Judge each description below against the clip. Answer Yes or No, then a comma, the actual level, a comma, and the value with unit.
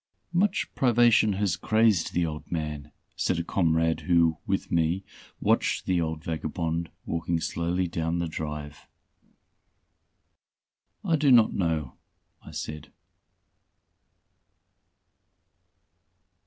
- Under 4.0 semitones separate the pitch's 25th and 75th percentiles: Yes, average, 3.3 semitones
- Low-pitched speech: Yes, very low, 85 Hz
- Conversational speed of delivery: No, slow, 100 wpm